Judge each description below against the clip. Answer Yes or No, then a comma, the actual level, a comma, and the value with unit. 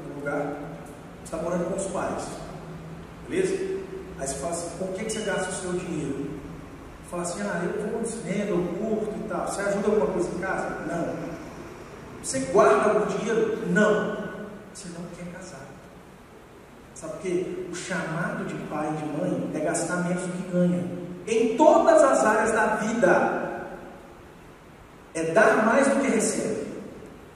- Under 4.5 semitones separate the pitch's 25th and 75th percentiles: Yes, average, 3.6 semitones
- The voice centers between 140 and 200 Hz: Yes, high, 190 Hz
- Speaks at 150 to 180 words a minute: Yes, average, 160 wpm